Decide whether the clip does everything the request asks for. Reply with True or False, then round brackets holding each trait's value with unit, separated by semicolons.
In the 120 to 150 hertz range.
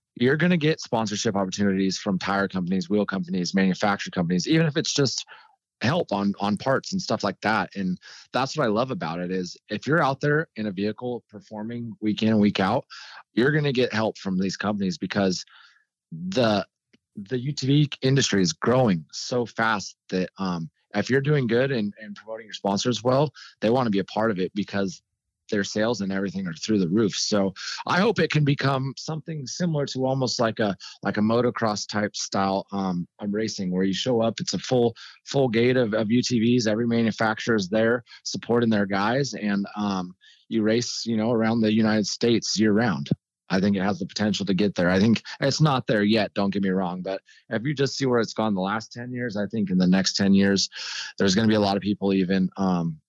False (110 Hz)